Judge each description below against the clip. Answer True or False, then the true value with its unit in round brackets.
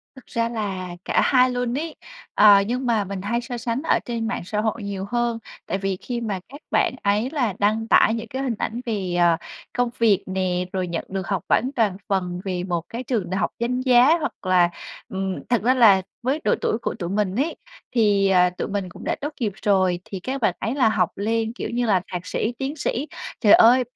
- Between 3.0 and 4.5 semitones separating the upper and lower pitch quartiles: True (4.2 semitones)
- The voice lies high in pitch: True (220 Hz)